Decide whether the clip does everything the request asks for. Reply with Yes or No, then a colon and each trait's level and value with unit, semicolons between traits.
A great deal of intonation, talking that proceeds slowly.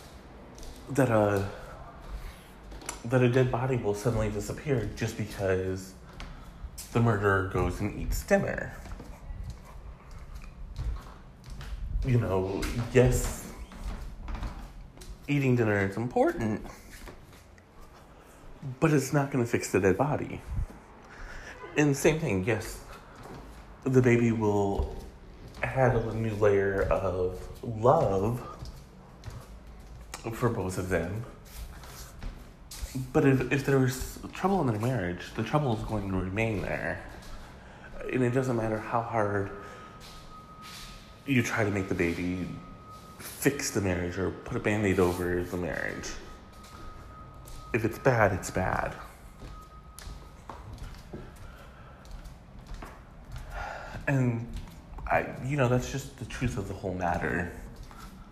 Yes: wide, 6.7 semitones; slow, 110 wpm